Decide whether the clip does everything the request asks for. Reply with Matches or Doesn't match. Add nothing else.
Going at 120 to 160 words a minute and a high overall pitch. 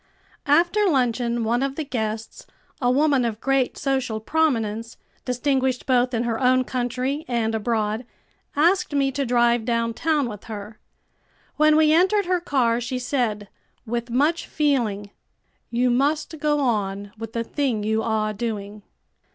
Matches